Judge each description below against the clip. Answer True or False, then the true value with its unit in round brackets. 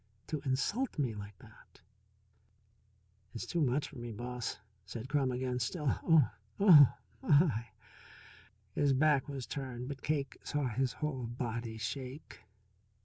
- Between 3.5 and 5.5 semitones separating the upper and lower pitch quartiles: True (3.9 semitones)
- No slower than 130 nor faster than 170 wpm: True (140 wpm)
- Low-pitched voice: True (130 Hz)